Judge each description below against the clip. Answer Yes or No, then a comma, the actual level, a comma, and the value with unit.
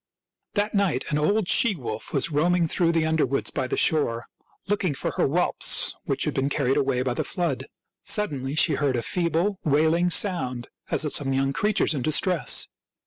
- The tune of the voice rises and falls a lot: No, average, 4.8 semitones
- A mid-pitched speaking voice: Yes, medium, 155 Hz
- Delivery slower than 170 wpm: No, average, 185 wpm